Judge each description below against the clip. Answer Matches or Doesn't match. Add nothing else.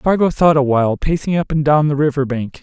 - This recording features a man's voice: Matches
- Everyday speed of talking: Doesn't match